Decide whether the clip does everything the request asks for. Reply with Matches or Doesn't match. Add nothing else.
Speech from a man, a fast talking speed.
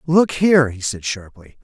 Doesn't match